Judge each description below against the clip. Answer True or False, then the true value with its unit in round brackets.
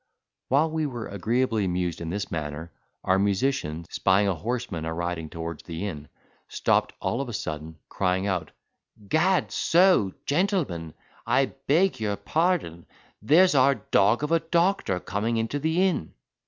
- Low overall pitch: True (105 Hz)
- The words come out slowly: False (155 wpm)